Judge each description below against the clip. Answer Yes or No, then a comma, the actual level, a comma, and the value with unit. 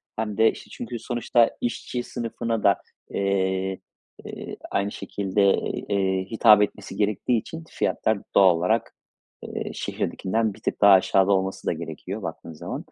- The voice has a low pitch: Yes, low, 100 Hz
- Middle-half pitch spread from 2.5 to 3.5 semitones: Yes, average, 2.8 semitones